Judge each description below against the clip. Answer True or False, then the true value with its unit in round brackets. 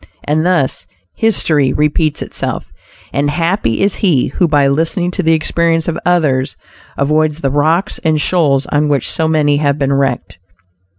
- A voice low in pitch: False (155 Hz)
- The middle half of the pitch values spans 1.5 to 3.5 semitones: True (2.9 semitones)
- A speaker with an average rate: True (160 wpm)